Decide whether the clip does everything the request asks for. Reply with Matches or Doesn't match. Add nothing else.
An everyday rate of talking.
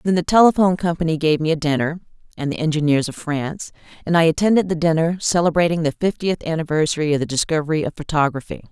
Matches